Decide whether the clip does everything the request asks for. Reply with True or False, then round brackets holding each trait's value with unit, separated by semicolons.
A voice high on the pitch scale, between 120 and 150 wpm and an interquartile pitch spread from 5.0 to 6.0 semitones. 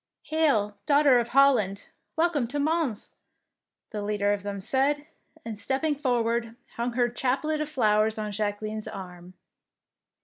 True (235 Hz; 140 wpm; 5.3 semitones)